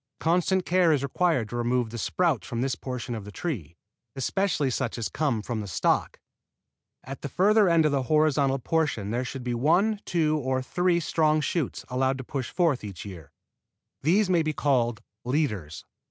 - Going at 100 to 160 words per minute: No, average, 185 wpm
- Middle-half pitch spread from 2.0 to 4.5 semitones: No, average, 5.3 semitones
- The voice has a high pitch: No, low, 135 Hz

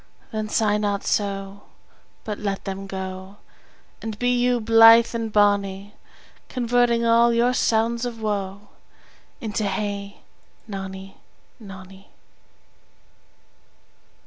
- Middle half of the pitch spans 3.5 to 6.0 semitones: No, average, 2.7 semitones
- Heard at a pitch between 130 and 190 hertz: No, high, 210 Hz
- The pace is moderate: No, slow, 100 wpm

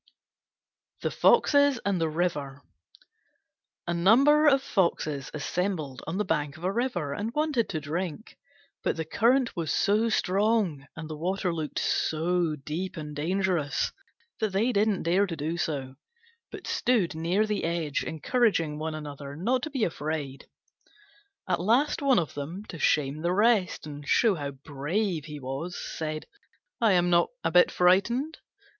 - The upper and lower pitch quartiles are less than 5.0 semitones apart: No, wide, 5.5 semitones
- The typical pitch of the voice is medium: Yes, medium, 175 Hz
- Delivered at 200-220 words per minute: No, average, 155 wpm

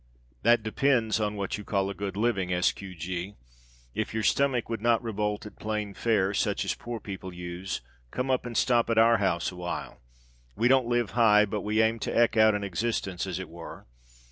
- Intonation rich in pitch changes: No, average, 3.4 semitones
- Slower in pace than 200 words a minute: No, fast, 205 wpm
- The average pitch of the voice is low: Yes, low, 105 Hz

